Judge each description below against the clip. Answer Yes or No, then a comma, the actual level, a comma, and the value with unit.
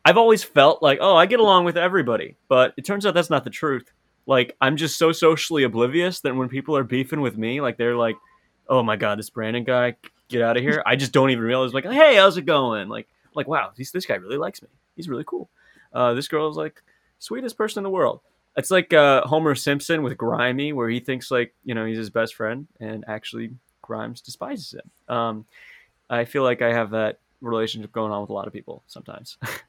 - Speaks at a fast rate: Yes, fast, 230 wpm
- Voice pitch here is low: Yes, low, 130 Hz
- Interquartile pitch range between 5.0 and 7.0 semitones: Yes, average, 5.3 semitones